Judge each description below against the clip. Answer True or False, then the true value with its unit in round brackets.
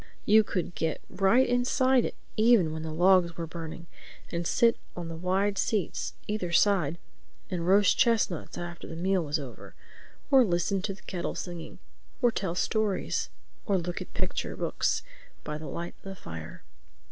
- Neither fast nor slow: True (165 wpm)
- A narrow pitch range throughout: False (3.7 semitones)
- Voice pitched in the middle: True (180 Hz)